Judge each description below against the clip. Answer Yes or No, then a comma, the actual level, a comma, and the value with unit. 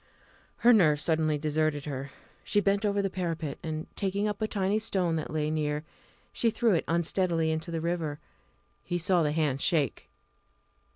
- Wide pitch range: No, average, 4.1 semitones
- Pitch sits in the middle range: Yes, medium, 165 Hz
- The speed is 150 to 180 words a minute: Yes, average, 170 wpm